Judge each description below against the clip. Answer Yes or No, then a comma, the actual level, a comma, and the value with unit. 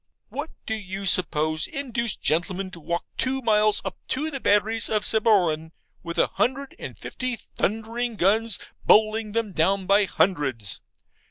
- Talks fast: No, average, 150 wpm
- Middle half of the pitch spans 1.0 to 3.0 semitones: No, average, 4.2 semitones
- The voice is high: Yes, high, 210 Hz